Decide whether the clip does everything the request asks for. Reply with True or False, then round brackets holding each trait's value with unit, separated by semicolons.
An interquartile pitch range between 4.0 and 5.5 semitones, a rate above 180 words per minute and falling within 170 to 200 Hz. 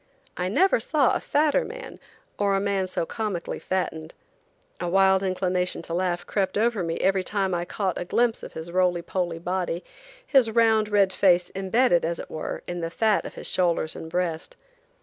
False (2.9 semitones; 190 wpm; 185 Hz)